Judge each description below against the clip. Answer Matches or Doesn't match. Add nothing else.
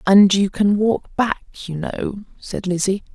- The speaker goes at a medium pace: Matches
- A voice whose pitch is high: Matches